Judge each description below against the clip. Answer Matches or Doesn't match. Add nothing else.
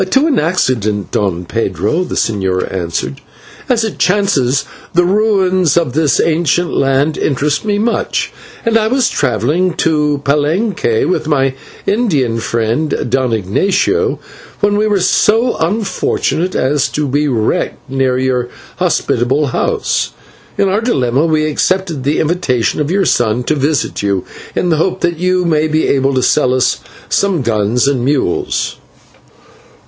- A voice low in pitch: Doesn't match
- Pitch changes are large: Matches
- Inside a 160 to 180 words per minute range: Doesn't match